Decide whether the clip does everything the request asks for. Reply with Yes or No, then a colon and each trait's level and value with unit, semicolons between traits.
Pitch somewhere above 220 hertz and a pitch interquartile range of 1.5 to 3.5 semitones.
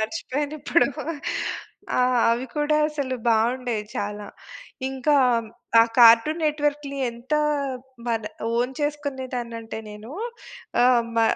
No: very high, 255 Hz; average, 4.2 semitones